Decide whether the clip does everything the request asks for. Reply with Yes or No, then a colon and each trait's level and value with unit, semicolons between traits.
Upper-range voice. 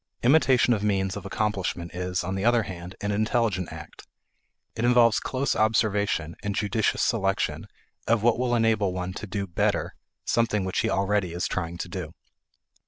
No: low, 100 Hz